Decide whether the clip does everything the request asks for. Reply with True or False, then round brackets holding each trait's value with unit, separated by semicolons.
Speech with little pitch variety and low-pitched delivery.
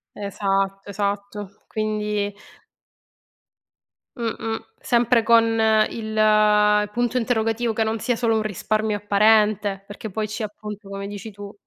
False (1.5 semitones; 210 Hz)